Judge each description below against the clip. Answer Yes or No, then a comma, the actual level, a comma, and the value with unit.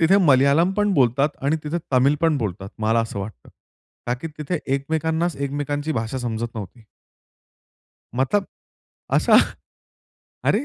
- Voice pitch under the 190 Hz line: Yes, medium, 140 Hz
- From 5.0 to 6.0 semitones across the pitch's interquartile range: Yes, wide, 5.5 semitones